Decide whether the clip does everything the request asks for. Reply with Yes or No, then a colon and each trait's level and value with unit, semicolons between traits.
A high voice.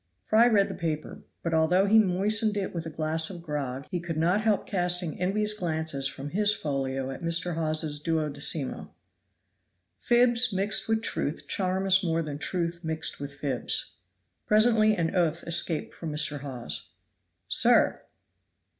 No: medium, 170 Hz